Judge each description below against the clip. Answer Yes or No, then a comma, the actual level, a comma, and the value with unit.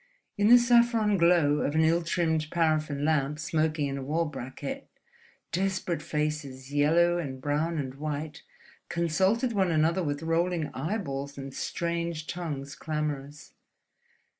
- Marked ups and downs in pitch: No, average, 3.0 semitones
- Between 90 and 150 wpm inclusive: Yes, slow, 135 wpm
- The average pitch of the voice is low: No, medium, 155 Hz